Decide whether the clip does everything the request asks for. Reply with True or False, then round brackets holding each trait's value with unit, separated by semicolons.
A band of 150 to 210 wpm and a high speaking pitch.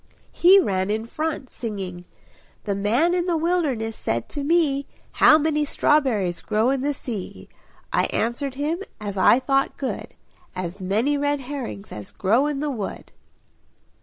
True (155 wpm; 260 Hz)